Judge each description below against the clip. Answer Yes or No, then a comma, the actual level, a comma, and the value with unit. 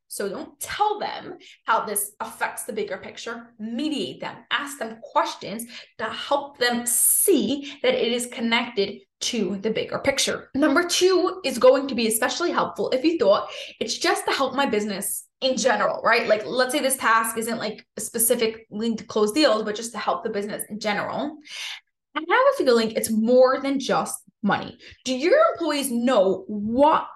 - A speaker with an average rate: Yes, average, 185 wpm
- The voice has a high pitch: Yes, high, 245 Hz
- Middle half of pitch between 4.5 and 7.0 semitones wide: Yes, average, 5.0 semitones